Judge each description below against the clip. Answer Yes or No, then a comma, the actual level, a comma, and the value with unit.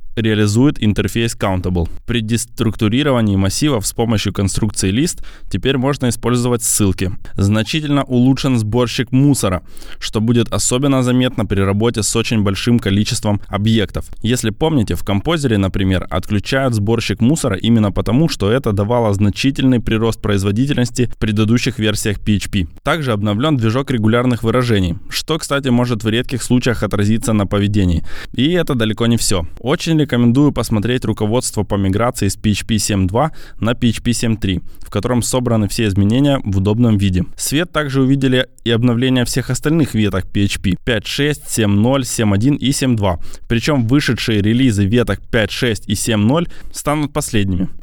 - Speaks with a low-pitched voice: Yes, low, 115 Hz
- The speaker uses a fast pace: No, average, 140 wpm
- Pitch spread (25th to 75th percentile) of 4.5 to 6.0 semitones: No, average, 3.9 semitones